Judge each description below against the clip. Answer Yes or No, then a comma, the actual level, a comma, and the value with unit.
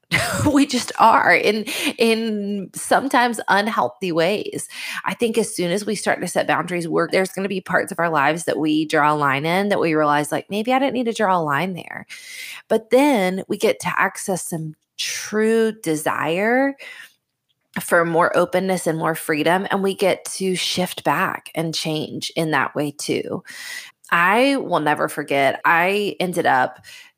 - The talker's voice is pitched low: No, medium, 185 Hz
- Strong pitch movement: Yes, wide, 6.0 semitones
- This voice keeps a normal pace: Yes, average, 175 wpm